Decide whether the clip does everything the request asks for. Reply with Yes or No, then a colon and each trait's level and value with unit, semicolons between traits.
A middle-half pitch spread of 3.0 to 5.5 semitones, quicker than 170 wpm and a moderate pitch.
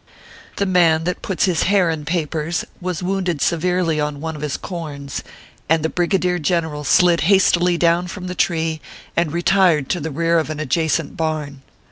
No: narrow, 2.5 semitones; average, 180 wpm; medium, 165 Hz